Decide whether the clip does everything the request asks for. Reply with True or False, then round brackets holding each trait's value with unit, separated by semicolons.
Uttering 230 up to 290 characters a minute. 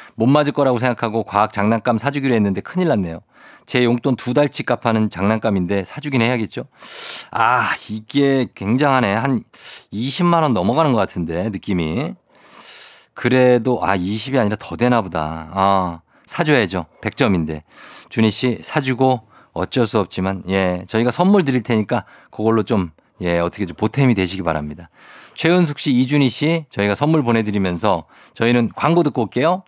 False (325 characters per minute)